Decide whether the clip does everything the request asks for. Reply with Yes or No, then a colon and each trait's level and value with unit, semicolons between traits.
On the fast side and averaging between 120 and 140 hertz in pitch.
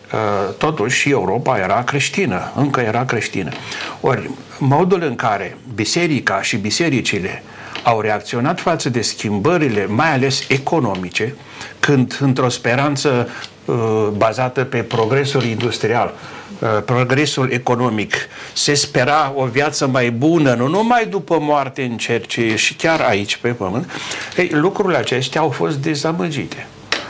No: average, 120 wpm; low, 130 Hz